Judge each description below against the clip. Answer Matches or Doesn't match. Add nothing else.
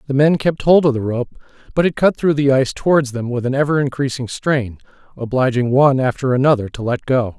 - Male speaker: Matches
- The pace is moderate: Doesn't match